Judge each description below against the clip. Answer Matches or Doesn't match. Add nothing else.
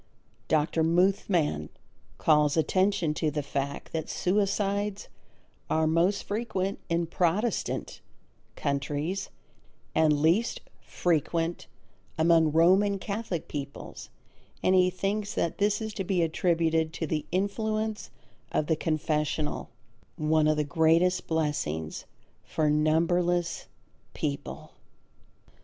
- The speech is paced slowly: Matches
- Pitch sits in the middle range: Matches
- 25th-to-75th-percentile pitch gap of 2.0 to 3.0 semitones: Doesn't match